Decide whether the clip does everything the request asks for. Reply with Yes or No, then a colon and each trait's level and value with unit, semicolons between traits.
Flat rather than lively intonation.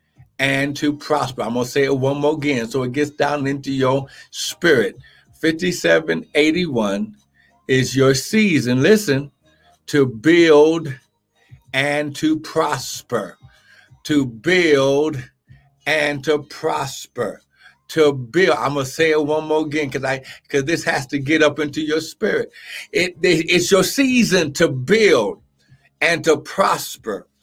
No: average, 3.0 semitones